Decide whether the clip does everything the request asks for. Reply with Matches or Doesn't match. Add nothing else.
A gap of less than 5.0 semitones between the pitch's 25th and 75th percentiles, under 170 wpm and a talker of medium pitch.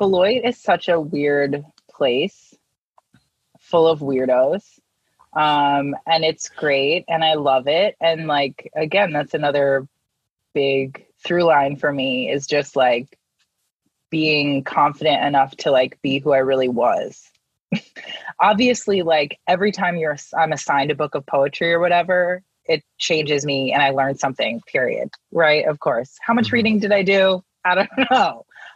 Matches